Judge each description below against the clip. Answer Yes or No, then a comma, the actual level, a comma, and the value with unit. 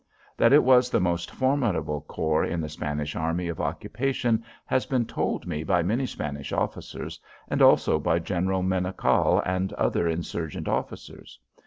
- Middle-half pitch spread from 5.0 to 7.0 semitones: Yes, wide, 5.5 semitones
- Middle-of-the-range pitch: No, very low, 90 Hz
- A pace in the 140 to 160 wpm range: Yes, average, 155 wpm